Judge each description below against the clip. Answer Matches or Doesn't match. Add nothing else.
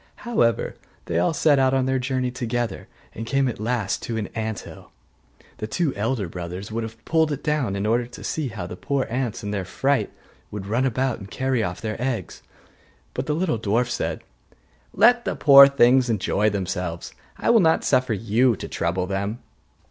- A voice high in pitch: Doesn't match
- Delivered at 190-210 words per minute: Matches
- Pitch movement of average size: Matches